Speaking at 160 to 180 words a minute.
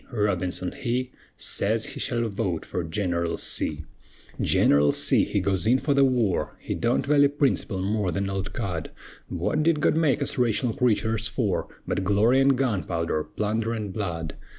Yes: average, 170 wpm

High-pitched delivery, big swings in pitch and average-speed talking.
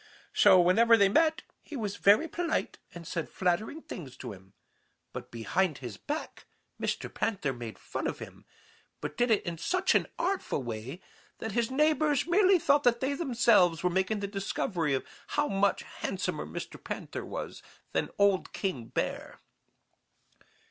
Yes: high, 200 Hz; wide, 8.7 semitones; average, 160 wpm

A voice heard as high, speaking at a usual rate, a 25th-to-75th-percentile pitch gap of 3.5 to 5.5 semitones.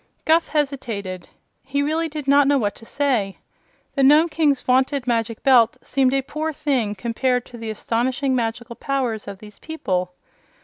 Yes: very high, 260 Hz; average, 165 wpm; average, 3.9 semitones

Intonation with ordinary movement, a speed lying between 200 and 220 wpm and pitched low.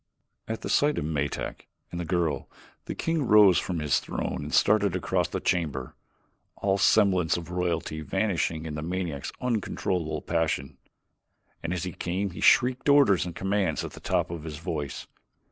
No: average, 3.8 semitones; average, 165 wpm; very low, 90 Hz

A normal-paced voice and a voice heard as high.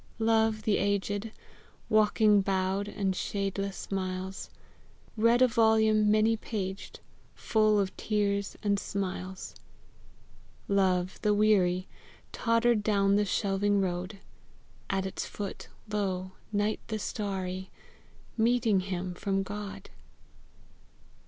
No: slow, 105 wpm; high, 200 Hz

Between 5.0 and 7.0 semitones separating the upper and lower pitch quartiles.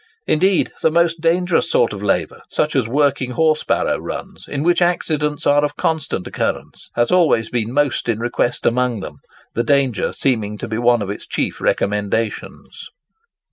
Yes: wide, 5.6 semitones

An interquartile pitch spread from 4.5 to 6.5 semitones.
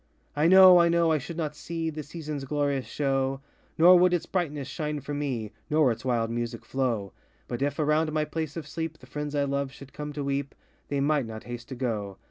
No: average, 2.9 semitones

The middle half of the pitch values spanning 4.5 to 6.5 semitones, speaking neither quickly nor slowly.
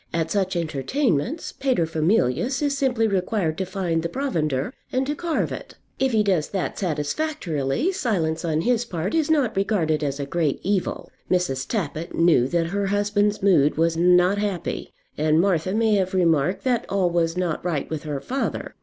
Yes: wide, 5.5 semitones; average, 170 wpm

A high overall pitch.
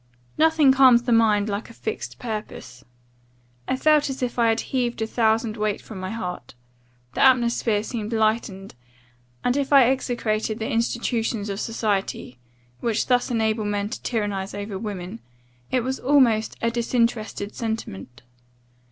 Yes: high, 225 Hz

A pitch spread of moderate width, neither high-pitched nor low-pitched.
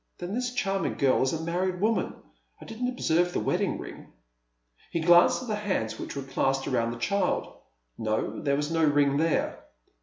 No: wide, 6.2 semitones; medium, 165 Hz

